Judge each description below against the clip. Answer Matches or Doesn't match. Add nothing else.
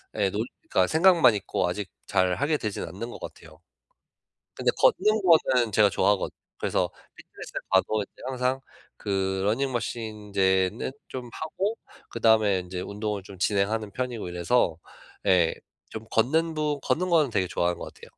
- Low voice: Matches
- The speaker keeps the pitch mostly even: Doesn't match